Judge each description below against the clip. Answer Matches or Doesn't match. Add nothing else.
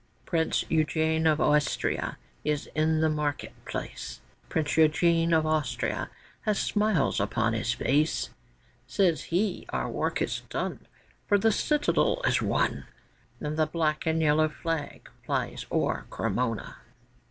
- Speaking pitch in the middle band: Matches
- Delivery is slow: Matches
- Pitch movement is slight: Matches